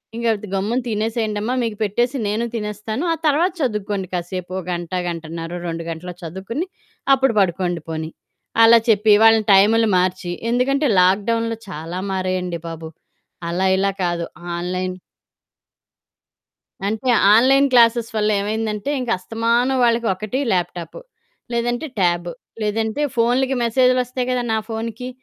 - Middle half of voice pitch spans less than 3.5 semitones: No, average, 4.5 semitones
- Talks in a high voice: Yes, high, 215 Hz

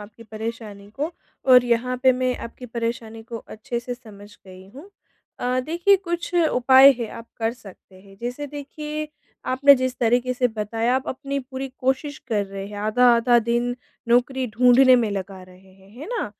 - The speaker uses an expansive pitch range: No, average, 3.2 semitones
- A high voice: Yes, high, 245 Hz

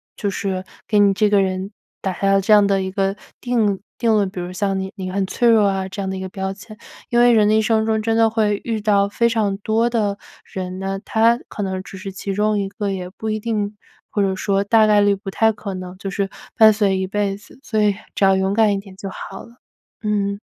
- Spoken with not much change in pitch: Yes, narrow, 2.0 semitones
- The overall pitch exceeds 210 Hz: No, high, 200 Hz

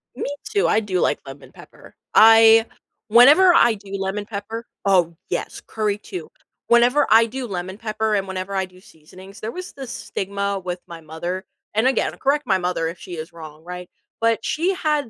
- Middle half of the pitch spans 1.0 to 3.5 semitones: No, average, 4.1 semitones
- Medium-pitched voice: No, high, 205 Hz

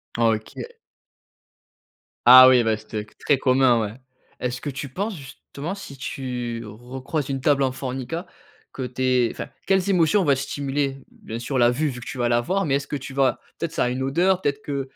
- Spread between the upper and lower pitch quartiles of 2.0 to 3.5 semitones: Yes, average, 2.7 semitones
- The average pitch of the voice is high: No, low, 135 Hz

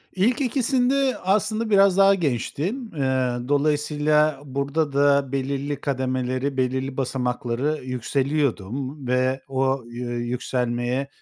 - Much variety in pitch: No, average, 3.3 semitones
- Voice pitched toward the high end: No, medium, 140 Hz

